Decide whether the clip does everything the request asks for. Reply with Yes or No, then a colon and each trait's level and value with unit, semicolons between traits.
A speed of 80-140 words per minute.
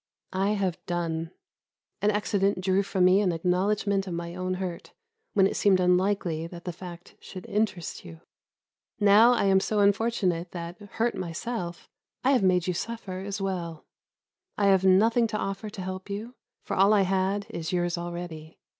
No: average, 170 wpm